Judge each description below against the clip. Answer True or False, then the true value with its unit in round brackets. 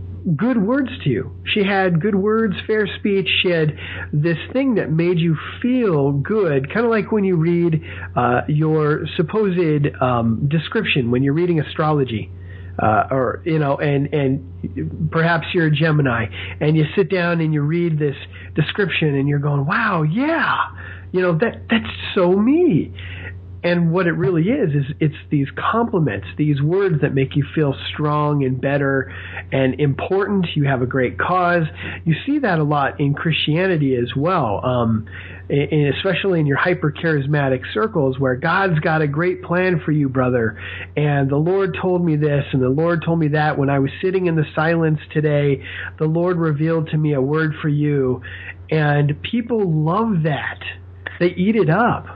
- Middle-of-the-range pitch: True (155 Hz)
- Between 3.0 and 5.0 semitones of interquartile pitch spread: True (4.6 semitones)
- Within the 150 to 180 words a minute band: True (175 wpm)